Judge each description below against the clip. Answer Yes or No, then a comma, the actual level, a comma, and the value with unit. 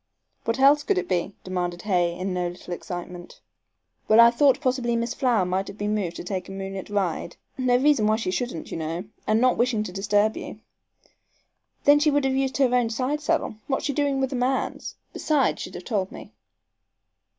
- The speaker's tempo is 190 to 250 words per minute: Yes, fast, 205 wpm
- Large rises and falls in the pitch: Yes, wide, 6.0 semitones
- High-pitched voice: Yes, high, 225 Hz